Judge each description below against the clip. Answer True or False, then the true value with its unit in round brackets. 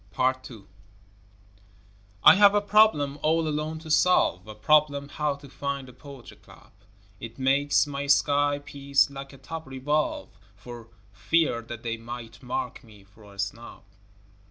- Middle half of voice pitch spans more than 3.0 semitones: True (4.0 semitones)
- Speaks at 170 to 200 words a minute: False (155 wpm)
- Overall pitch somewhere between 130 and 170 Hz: True (140 Hz)